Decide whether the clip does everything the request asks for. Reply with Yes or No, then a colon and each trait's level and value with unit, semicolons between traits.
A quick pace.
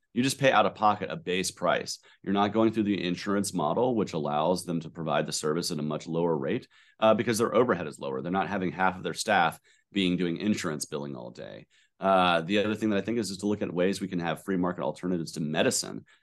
Yes: fast, 250 wpm